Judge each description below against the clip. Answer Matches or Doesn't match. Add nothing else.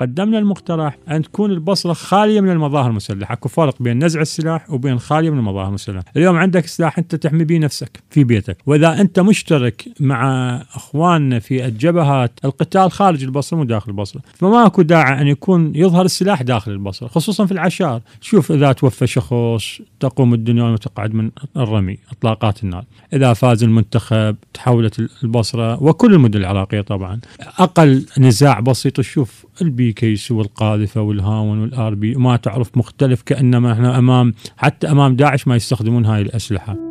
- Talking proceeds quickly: Matches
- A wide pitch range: Matches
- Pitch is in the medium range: Doesn't match